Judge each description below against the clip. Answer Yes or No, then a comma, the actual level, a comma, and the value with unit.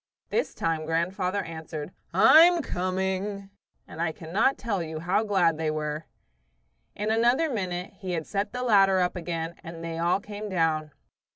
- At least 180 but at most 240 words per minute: No, average, 160 wpm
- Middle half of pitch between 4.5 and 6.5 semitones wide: No, average, 3.8 semitones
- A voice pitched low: No, medium, 180 Hz